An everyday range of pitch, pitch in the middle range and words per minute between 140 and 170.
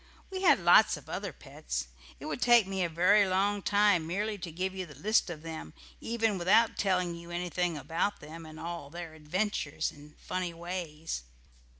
No: average, 3.9 semitones; medium, 175 Hz; average, 185 wpm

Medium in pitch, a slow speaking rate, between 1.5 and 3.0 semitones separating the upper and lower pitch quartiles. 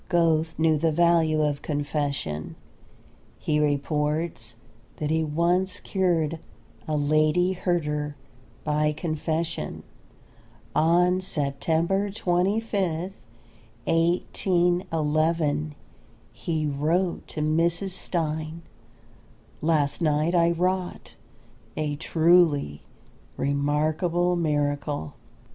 Yes: medium, 160 Hz; slow, 80 wpm; narrow, 2.6 semitones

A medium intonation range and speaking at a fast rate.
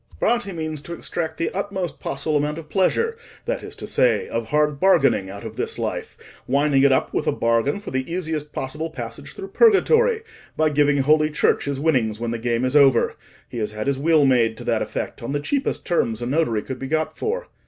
Yes: average, 4.7 semitones; fast, 215 wpm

